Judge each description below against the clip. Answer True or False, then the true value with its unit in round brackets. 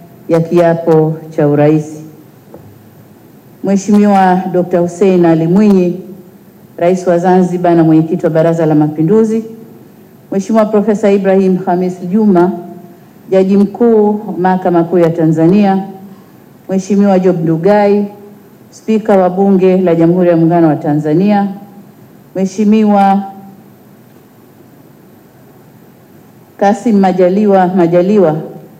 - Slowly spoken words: True (95 wpm)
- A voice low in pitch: False (185 Hz)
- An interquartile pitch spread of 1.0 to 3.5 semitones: True (2.7 semitones)